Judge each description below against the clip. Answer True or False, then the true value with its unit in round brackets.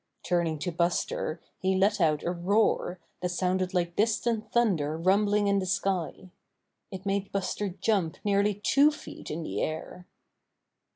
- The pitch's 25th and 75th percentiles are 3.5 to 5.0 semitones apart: False (2.9 semitones)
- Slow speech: False (150 wpm)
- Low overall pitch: False (185 Hz)